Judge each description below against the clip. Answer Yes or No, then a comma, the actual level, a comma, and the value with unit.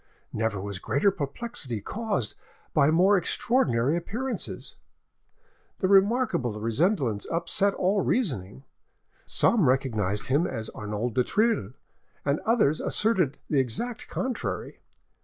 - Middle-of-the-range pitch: Yes, medium, 145 Hz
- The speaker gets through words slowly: Yes, slow, 110 wpm